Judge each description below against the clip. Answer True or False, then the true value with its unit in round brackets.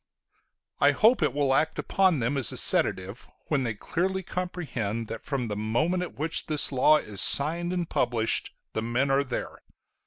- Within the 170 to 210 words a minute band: True (180 wpm)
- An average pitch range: False (6.7 semitones)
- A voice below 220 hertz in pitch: True (140 Hz)